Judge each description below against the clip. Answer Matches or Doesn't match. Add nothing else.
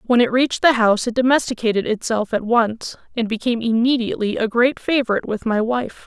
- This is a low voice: Doesn't match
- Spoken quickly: Doesn't match